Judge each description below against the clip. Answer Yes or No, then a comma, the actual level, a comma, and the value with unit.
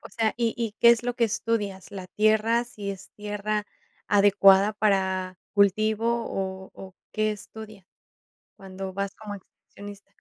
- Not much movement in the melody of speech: Yes, narrow, 2.0 semitones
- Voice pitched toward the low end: No, high, 205 Hz